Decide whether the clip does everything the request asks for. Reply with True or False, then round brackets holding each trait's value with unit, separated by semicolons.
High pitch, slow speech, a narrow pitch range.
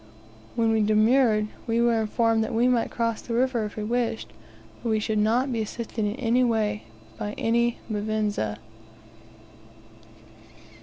True (225 Hz; 125 wpm; 1.8 semitones)